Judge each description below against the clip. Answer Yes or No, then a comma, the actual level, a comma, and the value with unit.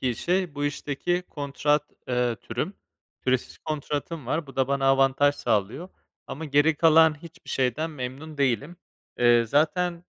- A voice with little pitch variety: No, average, 3.5 semitones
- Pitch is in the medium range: Yes, medium, 145 Hz